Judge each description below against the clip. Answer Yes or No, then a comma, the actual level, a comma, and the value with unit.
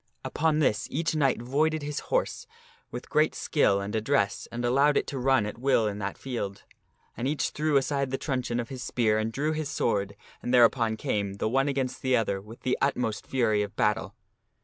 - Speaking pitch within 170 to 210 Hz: No, low, 125 Hz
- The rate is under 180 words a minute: No, average, 200 wpm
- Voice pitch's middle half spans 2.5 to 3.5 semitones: No, average, 4.4 semitones